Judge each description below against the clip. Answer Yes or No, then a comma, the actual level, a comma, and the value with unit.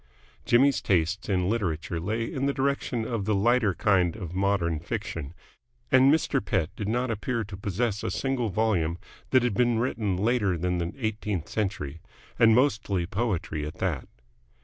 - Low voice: Yes, low, 105 Hz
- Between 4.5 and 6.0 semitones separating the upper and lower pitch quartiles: Yes, average, 4.8 semitones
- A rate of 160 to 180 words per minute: Yes, average, 165 wpm